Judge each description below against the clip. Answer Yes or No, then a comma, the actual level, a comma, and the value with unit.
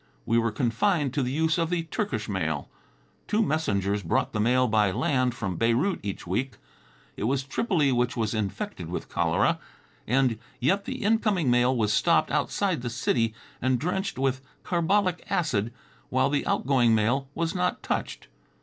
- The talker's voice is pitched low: Yes, low, 130 Hz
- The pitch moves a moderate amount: No, wide, 6.4 semitones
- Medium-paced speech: Yes, average, 165 wpm